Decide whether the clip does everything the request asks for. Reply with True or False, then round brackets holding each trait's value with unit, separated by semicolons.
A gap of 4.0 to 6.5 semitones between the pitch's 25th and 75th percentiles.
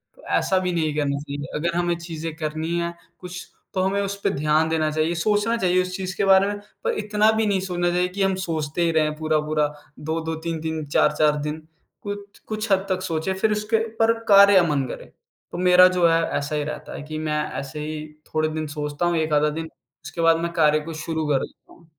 False (3.4 semitones)